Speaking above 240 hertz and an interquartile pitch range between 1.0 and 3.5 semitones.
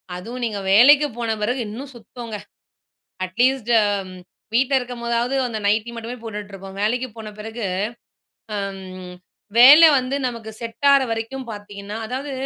No: high, 230 Hz; average, 3.2 semitones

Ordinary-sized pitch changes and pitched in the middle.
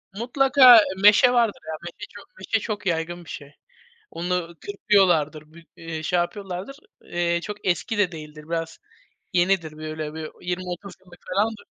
Yes: average, 4.0 semitones; medium, 175 Hz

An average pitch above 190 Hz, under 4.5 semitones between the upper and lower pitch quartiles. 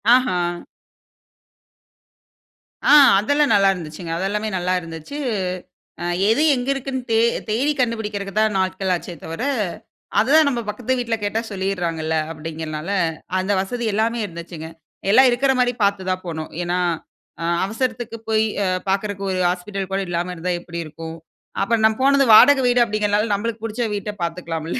No: high, 205 Hz; average, 4.9 semitones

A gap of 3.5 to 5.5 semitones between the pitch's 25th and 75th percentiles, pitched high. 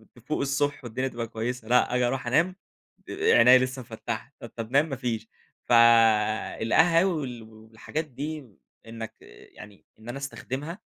No: average, 3.9 semitones; low, 125 Hz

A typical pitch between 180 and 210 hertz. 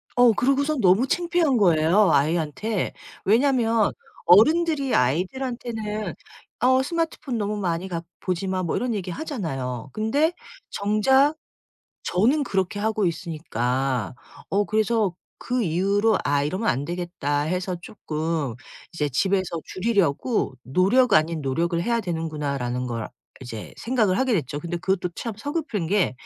Yes: high, 190 Hz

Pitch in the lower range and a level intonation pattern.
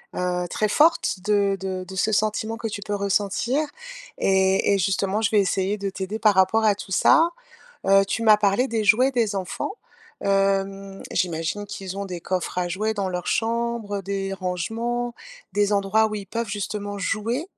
No: high, 200 Hz; narrow, 2.3 semitones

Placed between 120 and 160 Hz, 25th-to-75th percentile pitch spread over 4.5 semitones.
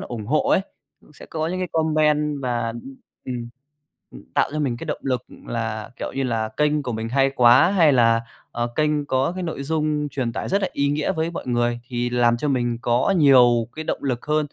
No: low, 135 Hz; average, 4.2 semitones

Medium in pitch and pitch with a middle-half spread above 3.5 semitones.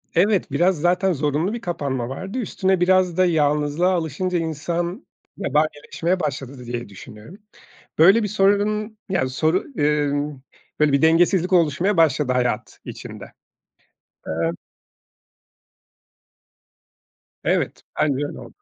Yes: medium, 165 Hz; average, 4.4 semitones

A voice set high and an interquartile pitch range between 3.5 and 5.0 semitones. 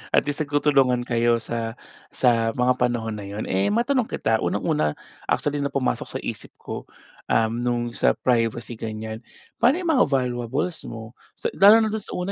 No: low, 120 Hz; average, 4.5 semitones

